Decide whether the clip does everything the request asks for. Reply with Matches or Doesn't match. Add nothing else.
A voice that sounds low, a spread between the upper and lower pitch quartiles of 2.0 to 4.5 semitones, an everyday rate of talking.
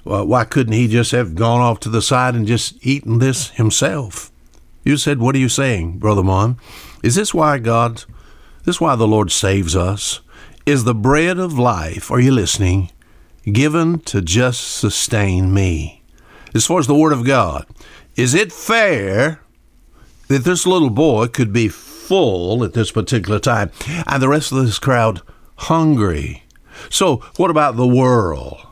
Doesn't match